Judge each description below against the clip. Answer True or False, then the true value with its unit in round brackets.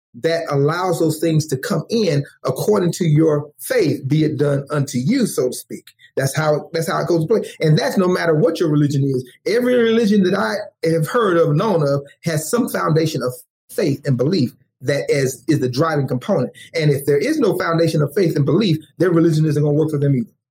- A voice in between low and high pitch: True (155 Hz)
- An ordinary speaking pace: False (220 wpm)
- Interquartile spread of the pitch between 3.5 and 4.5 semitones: False (2.9 semitones)